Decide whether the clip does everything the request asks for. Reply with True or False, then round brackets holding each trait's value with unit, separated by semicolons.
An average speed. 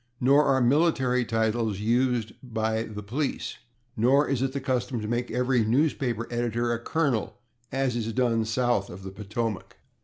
True (160 wpm)